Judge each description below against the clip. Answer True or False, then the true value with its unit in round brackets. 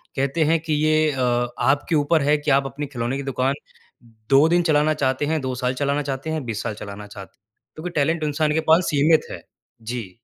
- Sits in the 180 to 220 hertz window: False (140 Hz)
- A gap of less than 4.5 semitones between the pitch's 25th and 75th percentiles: True (3.5 semitones)